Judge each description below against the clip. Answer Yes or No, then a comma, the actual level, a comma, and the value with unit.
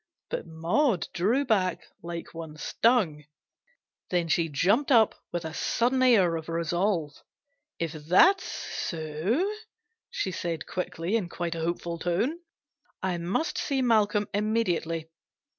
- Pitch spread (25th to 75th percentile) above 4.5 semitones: Yes, average, 5.3 semitones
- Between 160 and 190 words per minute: No, slow, 135 wpm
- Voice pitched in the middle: Yes, medium, 175 Hz